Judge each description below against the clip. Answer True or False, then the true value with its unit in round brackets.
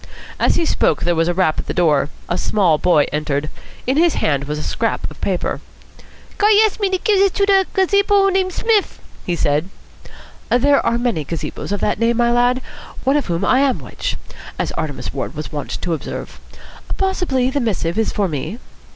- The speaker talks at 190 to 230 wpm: True (195 wpm)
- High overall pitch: True (225 Hz)